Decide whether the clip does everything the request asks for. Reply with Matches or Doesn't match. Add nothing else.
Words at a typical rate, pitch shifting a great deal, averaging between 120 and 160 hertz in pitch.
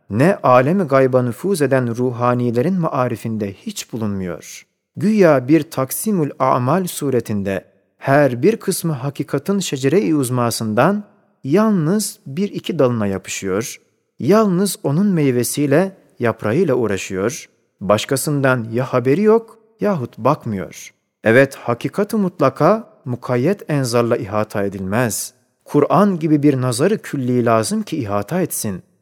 Matches